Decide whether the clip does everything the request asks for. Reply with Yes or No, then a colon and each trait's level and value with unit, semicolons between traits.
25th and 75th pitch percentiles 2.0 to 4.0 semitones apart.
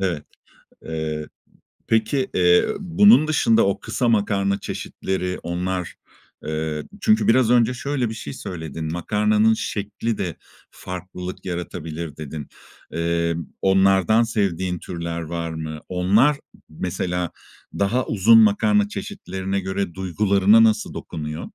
No: average, 4.7 semitones